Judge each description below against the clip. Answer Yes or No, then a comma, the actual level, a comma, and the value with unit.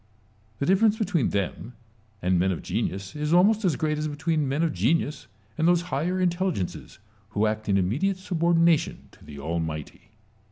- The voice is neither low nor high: Yes, medium, 150 Hz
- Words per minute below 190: Yes, average, 170 wpm